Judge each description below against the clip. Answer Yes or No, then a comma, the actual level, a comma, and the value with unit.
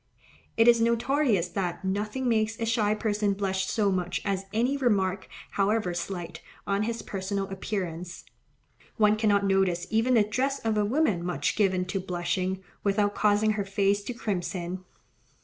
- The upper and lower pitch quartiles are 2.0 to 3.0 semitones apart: Yes, average, 2.7 semitones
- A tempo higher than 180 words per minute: No, average, 155 wpm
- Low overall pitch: No, high, 200 Hz